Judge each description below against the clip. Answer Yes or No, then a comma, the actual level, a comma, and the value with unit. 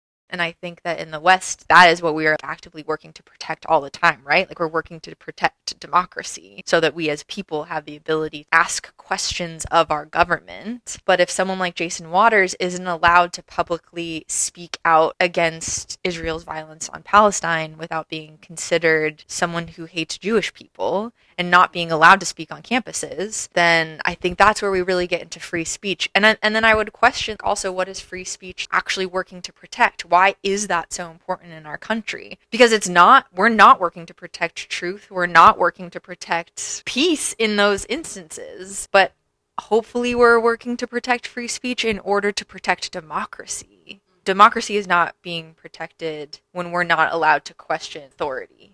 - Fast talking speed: No, average, 185 wpm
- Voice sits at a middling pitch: Yes, medium, 175 Hz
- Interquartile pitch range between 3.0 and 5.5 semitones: Yes, average, 3.4 semitones